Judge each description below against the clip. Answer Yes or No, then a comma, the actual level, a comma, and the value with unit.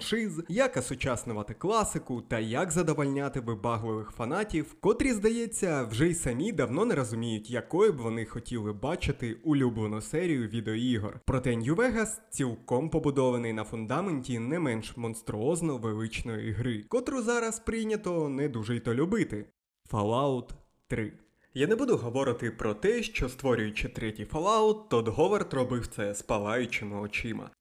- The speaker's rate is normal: Yes, average, 135 wpm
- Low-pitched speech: Yes, low, 125 Hz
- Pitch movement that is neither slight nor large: No, wide, 6.1 semitones